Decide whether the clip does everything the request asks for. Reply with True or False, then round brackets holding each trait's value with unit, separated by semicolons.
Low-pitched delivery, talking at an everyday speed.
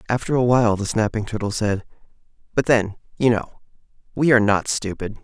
True (110 Hz; 170 wpm)